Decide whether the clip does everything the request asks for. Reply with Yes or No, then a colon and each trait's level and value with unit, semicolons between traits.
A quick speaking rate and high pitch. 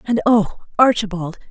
No: slow, 120 wpm; high, 205 Hz